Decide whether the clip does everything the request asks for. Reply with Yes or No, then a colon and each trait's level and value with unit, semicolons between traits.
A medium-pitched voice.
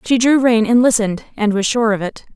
No: high, 225 Hz